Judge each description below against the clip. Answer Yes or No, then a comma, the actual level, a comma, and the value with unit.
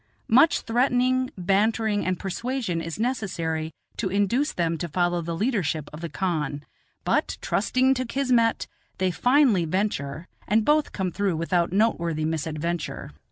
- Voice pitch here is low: No, high, 190 Hz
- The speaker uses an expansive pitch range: Yes, wide, 5.9 semitones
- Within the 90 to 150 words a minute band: Yes, average, 140 wpm